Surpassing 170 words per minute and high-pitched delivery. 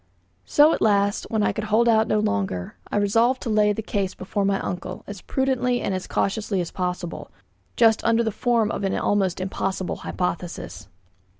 Yes: average, 185 wpm; high, 205 Hz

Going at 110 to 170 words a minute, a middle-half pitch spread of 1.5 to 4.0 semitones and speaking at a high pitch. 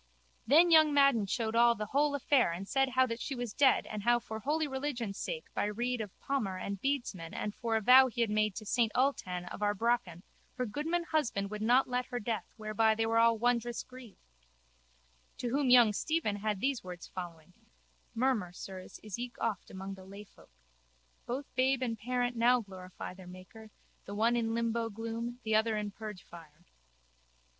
No: average, 185 wpm; average, 3.5 semitones; high, 230 Hz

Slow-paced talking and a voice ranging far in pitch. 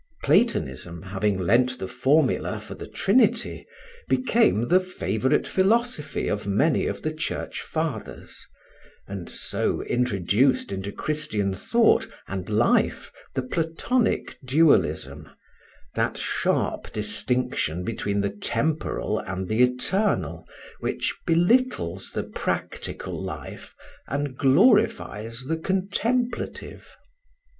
Yes: slow, 100 wpm; wide, 8.4 semitones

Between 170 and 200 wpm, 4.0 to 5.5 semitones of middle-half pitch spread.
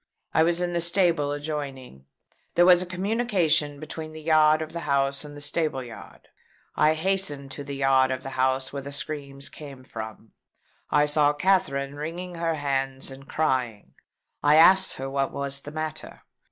No: average, 175 wpm; average, 3.0 semitones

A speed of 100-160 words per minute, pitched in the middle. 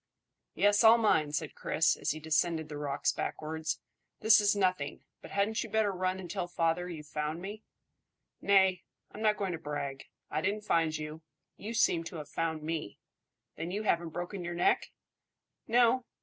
No: average, 175 wpm; medium, 175 Hz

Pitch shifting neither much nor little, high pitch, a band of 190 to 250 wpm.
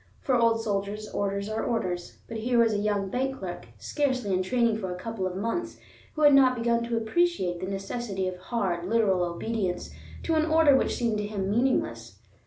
Yes: average, 4.0 semitones; high, 220 Hz; average, 195 wpm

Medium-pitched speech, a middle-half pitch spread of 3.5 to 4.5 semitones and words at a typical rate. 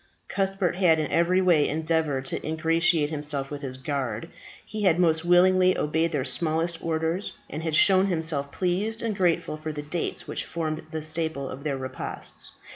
No: medium, 160 Hz; average, 3.0 semitones; average, 170 wpm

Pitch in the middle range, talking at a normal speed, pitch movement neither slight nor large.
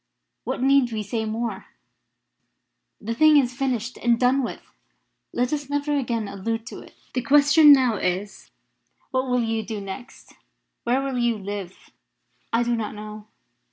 No: high, 240 Hz; average, 155 wpm; average, 3.7 semitones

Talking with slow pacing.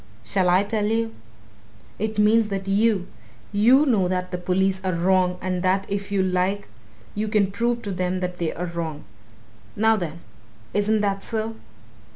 No: average, 170 wpm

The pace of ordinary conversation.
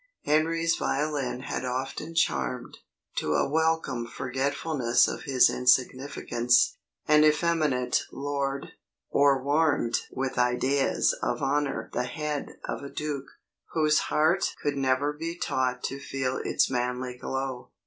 No: slow, 125 wpm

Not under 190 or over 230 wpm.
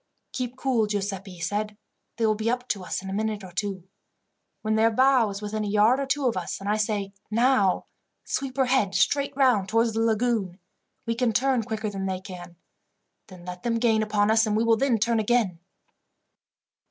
Yes: fast, 205 wpm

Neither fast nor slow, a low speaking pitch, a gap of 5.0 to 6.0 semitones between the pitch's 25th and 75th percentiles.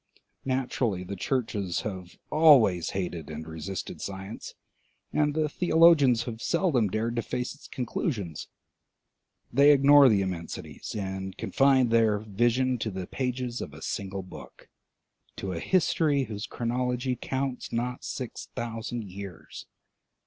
No: slow, 130 wpm; low, 115 Hz; average, 5.3 semitones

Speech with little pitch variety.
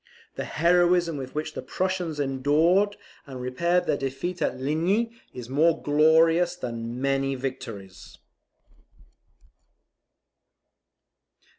No: average, 4.8 semitones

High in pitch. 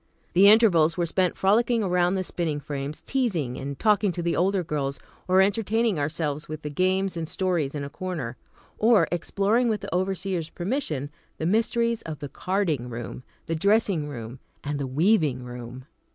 No: medium, 175 Hz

